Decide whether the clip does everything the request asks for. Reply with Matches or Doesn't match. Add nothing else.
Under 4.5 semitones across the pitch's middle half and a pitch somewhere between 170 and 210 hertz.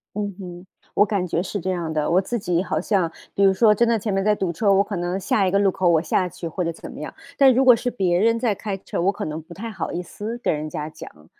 Matches